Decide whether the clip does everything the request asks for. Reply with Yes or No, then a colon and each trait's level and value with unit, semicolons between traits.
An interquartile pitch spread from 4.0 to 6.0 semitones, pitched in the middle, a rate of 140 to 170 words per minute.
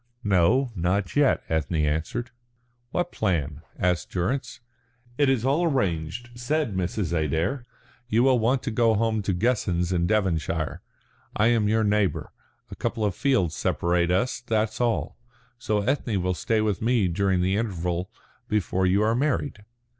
No: average, 5.2 semitones; low, 105 Hz; average, 155 wpm